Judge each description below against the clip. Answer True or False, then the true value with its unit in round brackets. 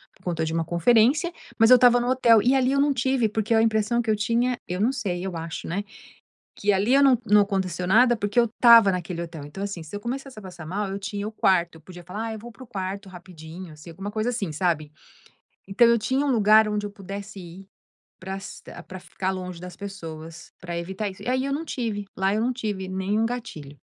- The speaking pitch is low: False (200 Hz)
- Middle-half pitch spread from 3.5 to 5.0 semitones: True (4.4 semitones)